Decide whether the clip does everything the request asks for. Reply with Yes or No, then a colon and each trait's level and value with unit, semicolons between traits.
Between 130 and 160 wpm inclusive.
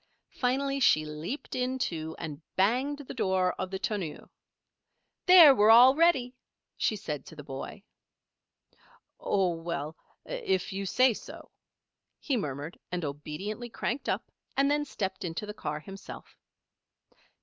Yes: average, 140 wpm